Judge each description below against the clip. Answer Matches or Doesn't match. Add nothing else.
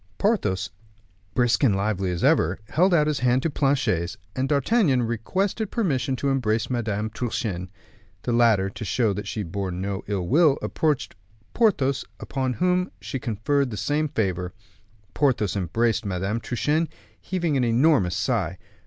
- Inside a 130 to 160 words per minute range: Matches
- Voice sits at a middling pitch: Doesn't match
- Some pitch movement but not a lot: Doesn't match